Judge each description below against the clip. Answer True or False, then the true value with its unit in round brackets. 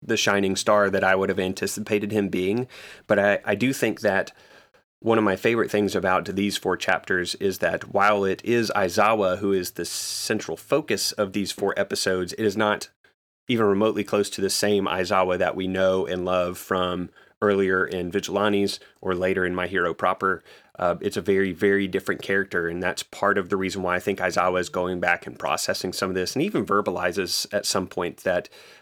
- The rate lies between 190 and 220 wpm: True (200 wpm)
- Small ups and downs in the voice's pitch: True (1.9 semitones)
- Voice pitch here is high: False (95 Hz)